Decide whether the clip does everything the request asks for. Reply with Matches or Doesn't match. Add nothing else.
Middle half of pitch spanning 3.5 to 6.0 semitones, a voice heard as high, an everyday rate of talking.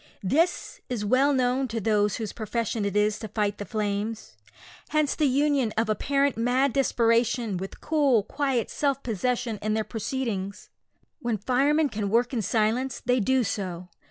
Matches